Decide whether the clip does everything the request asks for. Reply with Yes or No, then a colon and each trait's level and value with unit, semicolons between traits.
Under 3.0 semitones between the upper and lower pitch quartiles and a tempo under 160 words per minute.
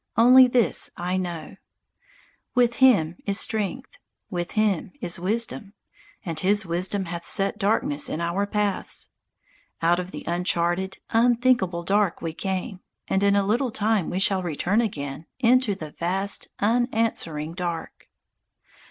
No: average, 4.2 semitones; slow, 135 wpm